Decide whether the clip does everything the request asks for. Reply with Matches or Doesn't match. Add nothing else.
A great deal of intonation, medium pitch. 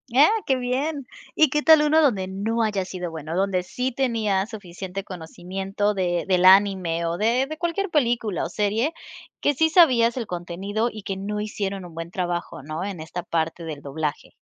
Doesn't match